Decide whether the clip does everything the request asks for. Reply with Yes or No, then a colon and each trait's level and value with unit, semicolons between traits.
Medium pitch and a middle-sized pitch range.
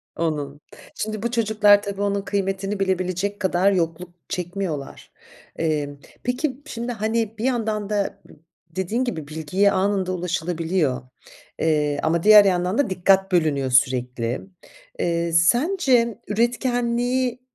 No: high, 195 Hz; average, 4.8 semitones